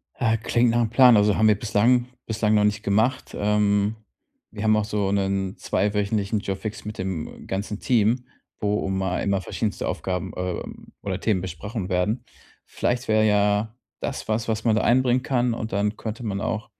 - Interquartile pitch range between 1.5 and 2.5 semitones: Yes, narrow, 2.1 semitones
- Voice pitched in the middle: No, low, 105 Hz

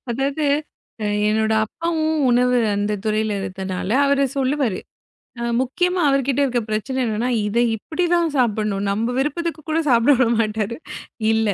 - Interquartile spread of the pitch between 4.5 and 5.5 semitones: Yes, average, 4.9 semitones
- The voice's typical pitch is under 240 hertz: No, high, 245 Hz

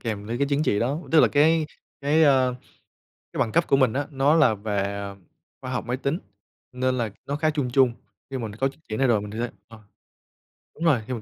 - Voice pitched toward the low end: Yes, low, 130 Hz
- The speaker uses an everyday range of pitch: Yes, average, 4.2 semitones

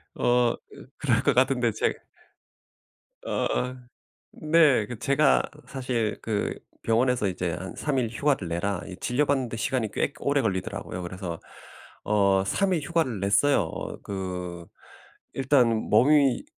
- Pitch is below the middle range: Yes, low, 120 Hz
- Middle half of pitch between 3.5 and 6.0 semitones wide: Yes, wide, 5.7 semitones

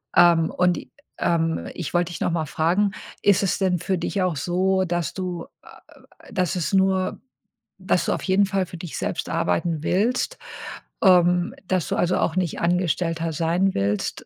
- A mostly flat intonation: Yes, narrow, 2.1 semitones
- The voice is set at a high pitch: No, medium, 175 Hz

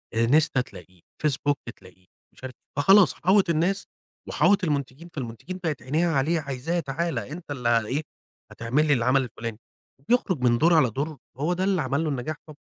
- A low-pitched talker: No, medium, 145 Hz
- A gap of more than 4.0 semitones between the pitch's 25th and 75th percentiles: Yes, average, 5.0 semitones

